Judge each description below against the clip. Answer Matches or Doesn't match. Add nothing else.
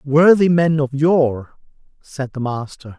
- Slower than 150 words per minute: Matches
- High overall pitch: Doesn't match